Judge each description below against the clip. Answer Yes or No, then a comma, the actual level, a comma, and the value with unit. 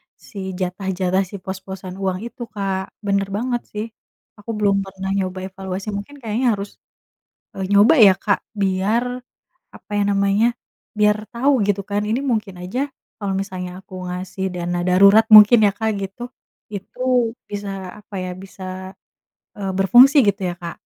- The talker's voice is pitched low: No, high, 195 Hz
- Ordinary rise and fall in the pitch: No, narrow, 1.9 semitones